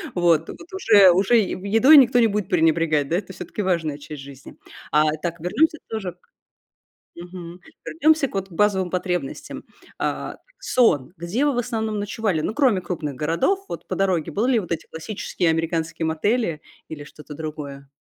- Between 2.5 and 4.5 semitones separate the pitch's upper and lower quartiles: No, average, 5.2 semitones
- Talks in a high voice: No, medium, 180 Hz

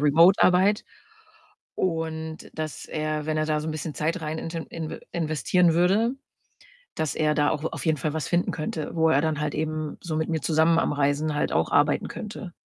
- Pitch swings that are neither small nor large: No, narrow, 1.5 semitones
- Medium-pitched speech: Yes, medium, 155 Hz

